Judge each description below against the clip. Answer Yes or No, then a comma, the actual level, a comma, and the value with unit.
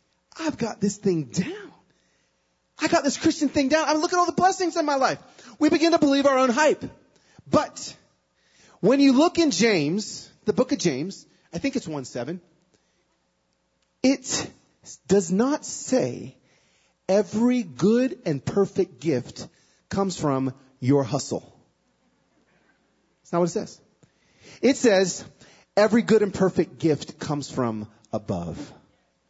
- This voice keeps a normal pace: Yes, average, 145 wpm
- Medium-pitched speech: No, high, 200 Hz